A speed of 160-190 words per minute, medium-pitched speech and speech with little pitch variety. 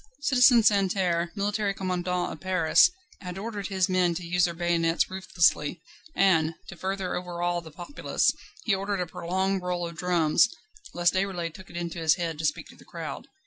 Yes: average, 180 wpm; medium, 180 Hz; narrow, 2.1 semitones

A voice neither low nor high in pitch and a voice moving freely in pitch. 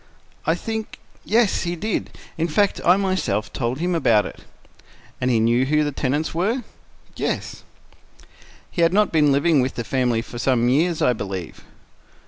Yes: medium, 150 Hz; wide, 6.3 semitones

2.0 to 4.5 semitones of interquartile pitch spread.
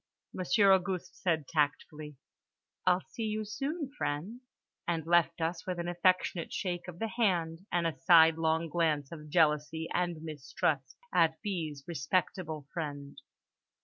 Yes: average, 2.9 semitones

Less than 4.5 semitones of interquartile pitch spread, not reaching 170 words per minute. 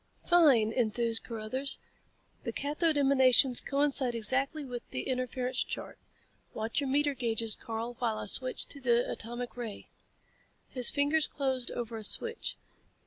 Yes: average, 3.2 semitones; average, 140 wpm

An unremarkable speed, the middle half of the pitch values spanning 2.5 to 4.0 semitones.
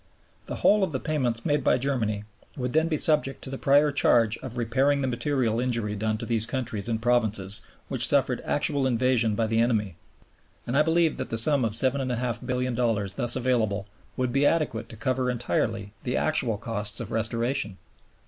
Yes: average, 180 wpm; average, 3.2 semitones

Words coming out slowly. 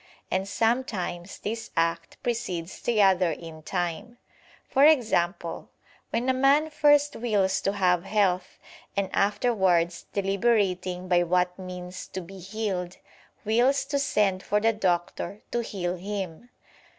Yes: slow, 130 wpm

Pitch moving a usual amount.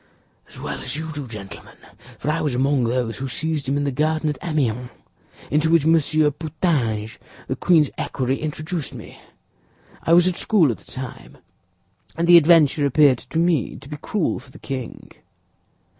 Yes: average, 3.5 semitones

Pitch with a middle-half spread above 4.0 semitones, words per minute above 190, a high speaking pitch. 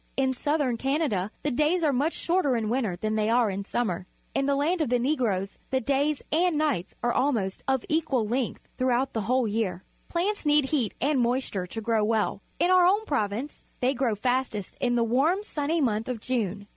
Yes: average, 5.1 semitones; average, 200 wpm; very high, 255 Hz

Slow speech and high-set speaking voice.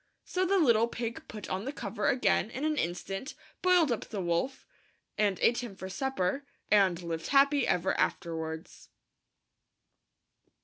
No: average, 145 wpm; high, 215 Hz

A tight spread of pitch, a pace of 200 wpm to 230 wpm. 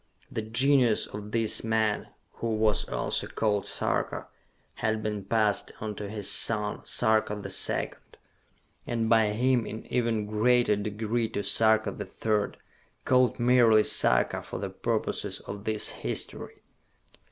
No: narrow, 1.6 semitones; average, 140 wpm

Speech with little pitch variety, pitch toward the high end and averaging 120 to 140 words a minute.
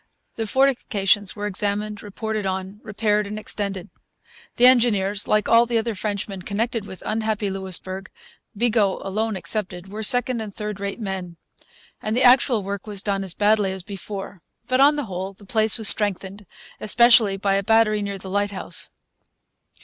No: narrow, 2.1 semitones; high, 205 Hz; average, 165 wpm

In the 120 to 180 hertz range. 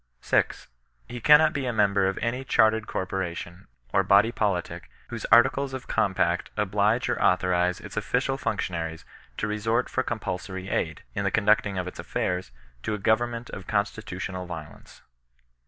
No: low, 100 Hz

